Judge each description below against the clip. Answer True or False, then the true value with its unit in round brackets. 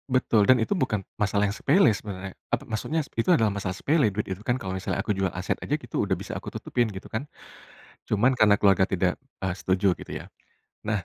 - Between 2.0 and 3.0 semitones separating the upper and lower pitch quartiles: False (4.0 semitones)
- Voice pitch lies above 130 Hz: False (105 Hz)